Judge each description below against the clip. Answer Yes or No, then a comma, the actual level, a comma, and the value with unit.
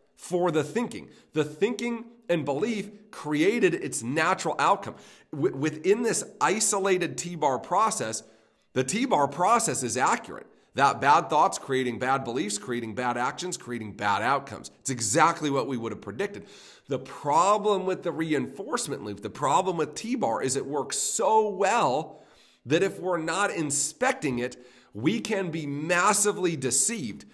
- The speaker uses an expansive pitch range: Yes, wide, 7.8 semitones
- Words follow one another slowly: No, average, 155 wpm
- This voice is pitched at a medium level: Yes, medium, 160 Hz